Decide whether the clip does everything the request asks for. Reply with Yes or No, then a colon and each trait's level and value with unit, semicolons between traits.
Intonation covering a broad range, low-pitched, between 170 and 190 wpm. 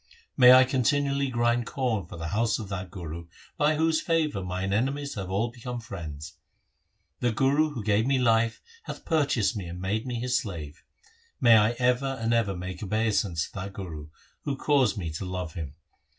Yes: wide, 5.7 semitones; low, 110 Hz; average, 185 wpm